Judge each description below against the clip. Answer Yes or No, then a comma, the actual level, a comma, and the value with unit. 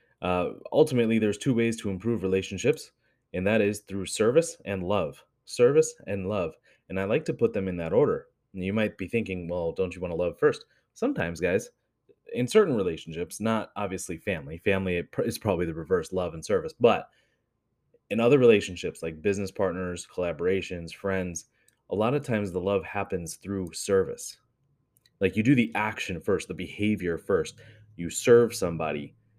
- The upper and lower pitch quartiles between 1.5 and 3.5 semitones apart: No, average, 4.6 semitones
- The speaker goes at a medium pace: Yes, average, 175 wpm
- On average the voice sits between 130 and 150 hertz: No, low, 100 Hz